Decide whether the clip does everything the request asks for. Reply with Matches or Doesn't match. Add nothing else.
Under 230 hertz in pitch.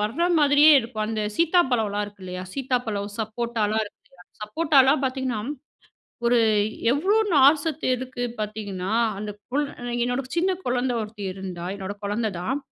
Doesn't match